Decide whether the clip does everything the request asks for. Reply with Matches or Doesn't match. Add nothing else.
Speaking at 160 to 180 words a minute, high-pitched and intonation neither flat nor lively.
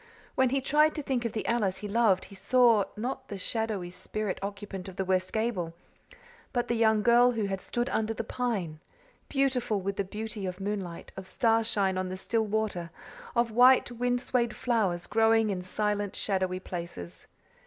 Matches